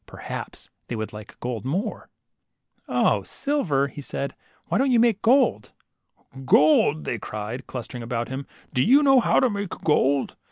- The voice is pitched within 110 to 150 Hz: Yes, medium, 140 Hz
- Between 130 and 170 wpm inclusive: Yes, average, 165 wpm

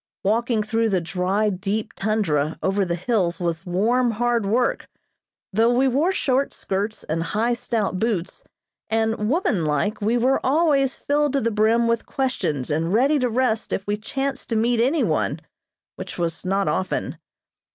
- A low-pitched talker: No, high, 220 Hz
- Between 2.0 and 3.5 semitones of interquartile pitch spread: No, average, 4.3 semitones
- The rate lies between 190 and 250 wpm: No, average, 160 wpm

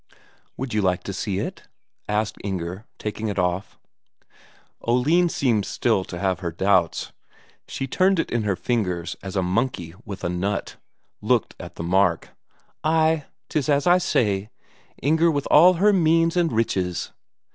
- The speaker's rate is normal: Yes, average, 155 wpm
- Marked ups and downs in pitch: Yes, wide, 8.3 semitones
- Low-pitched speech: Yes, low, 105 Hz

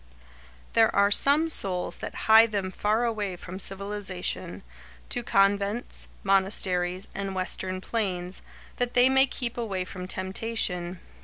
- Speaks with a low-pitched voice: No, high, 195 Hz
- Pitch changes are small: No, average, 3.2 semitones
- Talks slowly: Yes, slow, 125 wpm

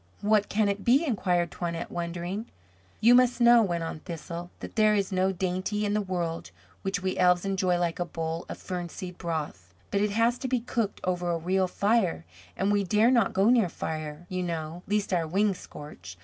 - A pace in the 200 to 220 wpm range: Yes, fast, 205 wpm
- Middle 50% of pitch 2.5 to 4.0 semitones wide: Yes, average, 3.4 semitones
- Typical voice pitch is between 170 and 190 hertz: Yes, medium, 185 Hz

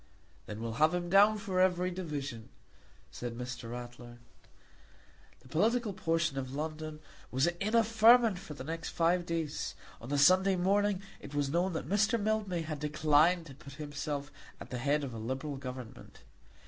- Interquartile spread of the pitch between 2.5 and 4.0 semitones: No, wide, 5.4 semitones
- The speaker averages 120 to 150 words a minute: No, average, 170 wpm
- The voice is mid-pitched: Yes, medium, 155 Hz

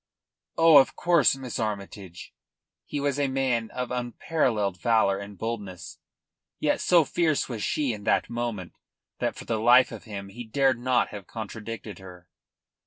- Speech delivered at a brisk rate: No, average, 160 wpm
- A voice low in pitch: Yes, low, 115 Hz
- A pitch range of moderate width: Yes, average, 4.5 semitones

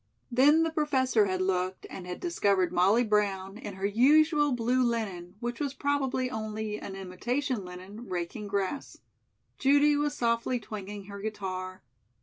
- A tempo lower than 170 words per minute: Yes, average, 145 wpm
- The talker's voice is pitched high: Yes, high, 215 Hz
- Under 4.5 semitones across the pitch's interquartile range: No, average, 5.3 semitones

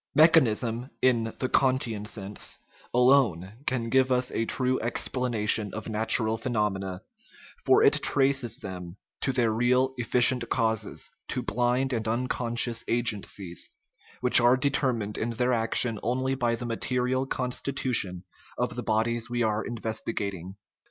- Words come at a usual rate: No, slow, 130 wpm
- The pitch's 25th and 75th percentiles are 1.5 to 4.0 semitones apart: Yes, narrow, 2.5 semitones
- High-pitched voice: No, low, 120 Hz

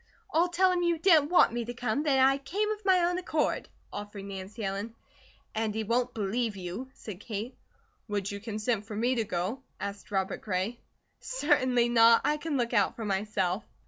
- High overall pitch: Yes, high, 230 Hz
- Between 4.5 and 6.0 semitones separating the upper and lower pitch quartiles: Yes, wide, 5.4 semitones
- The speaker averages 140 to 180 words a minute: No, average, 190 wpm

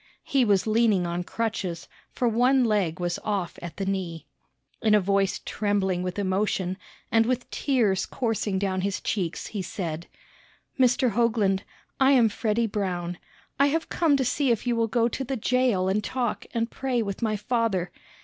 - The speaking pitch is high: Yes, high, 210 Hz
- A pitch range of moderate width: Yes, average, 4.1 semitones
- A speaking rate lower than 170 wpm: No, average, 175 wpm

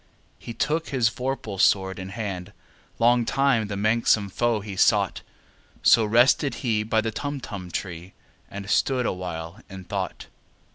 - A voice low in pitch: Yes, low, 110 Hz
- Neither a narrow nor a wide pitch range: Yes, average, 4.0 semitones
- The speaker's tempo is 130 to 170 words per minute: Yes, average, 145 wpm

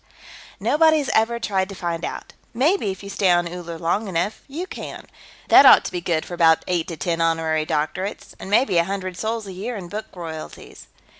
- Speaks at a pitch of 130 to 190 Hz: Yes, medium, 185 Hz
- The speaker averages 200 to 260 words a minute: Yes, fast, 205 wpm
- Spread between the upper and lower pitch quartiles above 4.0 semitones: Yes, average, 4.4 semitones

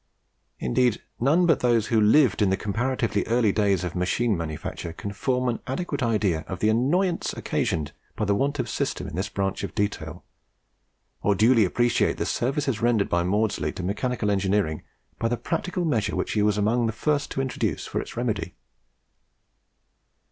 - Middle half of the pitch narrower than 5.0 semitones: Yes, average, 4.2 semitones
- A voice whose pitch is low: Yes, low, 110 Hz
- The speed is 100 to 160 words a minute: No, average, 175 wpm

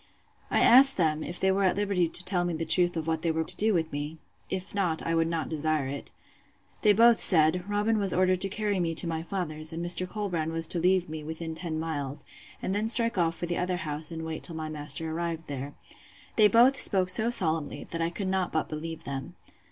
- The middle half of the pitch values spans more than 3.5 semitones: No, average, 3.0 semitones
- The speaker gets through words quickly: Yes, fast, 230 wpm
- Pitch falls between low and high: Yes, medium, 170 Hz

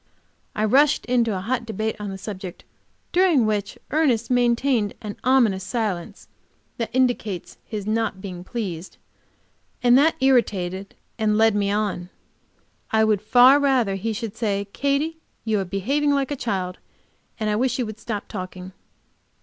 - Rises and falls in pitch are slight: No, average, 4.0 semitones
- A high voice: Yes, high, 220 Hz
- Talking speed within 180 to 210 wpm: No, average, 155 wpm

